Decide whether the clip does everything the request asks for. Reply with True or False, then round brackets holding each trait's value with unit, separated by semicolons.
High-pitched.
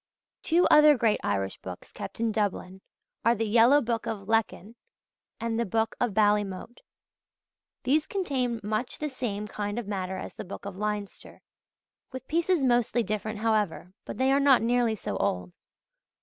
True (225 Hz)